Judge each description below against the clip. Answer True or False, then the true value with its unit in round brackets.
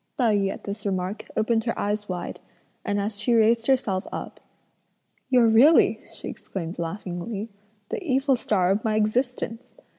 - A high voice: True (215 Hz)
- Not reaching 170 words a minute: True (155 wpm)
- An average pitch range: True (3.1 semitones)